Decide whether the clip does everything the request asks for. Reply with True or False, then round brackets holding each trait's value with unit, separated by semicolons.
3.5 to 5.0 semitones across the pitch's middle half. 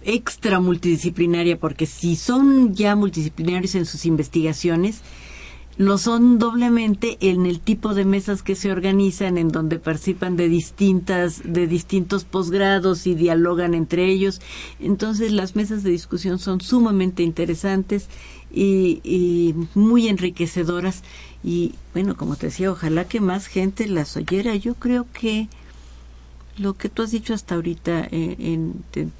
False (3.1 semitones)